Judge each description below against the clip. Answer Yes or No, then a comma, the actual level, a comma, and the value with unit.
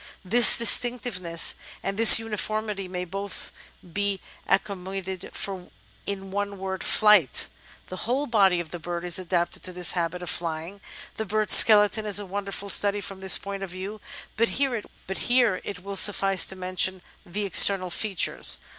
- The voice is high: Yes, high, 195 Hz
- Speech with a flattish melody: Yes, narrow, 2.3 semitones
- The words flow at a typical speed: Yes, average, 165 wpm